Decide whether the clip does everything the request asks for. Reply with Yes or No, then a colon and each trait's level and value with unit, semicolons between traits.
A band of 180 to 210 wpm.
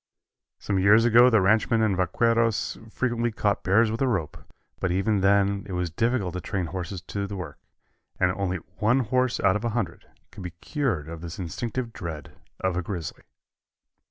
Yes: average, 185 wpm